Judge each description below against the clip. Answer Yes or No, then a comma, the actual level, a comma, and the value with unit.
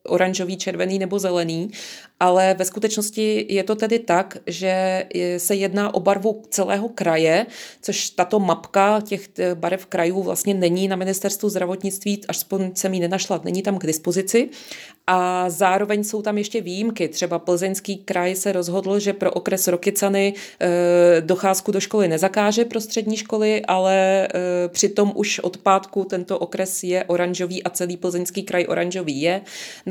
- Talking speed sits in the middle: Yes, average, 150 wpm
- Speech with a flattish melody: Yes, narrow, 2.1 semitones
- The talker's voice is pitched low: No, high, 190 Hz